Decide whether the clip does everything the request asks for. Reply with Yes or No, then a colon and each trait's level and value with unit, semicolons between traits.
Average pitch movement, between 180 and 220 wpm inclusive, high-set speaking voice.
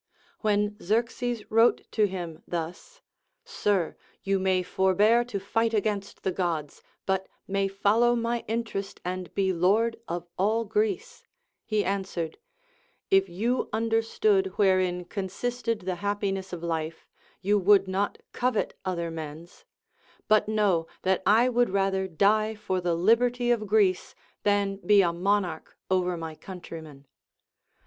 No: average, 3.4 semitones; slow, 135 wpm; high, 195 Hz